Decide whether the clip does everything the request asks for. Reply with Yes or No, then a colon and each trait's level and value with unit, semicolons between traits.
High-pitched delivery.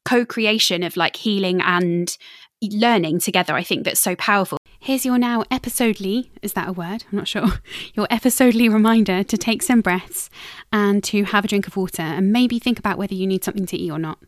Yes: high, 205 Hz